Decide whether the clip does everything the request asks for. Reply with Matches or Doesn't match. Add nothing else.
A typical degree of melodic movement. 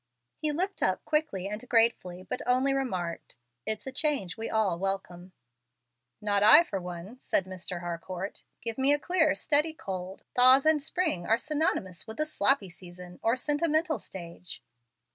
Doesn't match